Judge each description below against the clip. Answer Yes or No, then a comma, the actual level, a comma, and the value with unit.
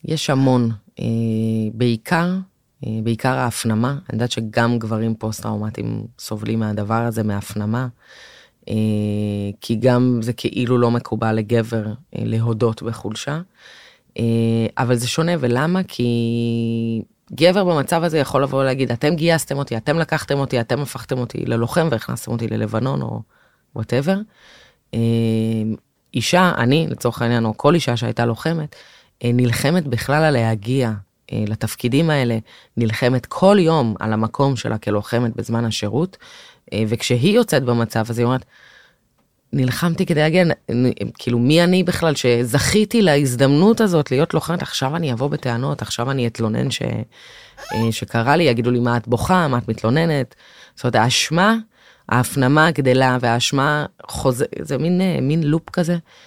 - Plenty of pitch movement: No, average, 4.7 semitones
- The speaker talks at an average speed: Yes, average, 130 wpm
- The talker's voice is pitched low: Yes, low, 125 Hz